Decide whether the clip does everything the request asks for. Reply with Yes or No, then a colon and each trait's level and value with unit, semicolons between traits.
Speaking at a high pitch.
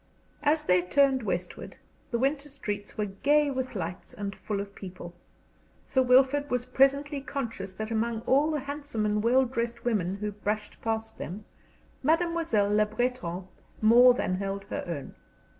Yes: high, 230 Hz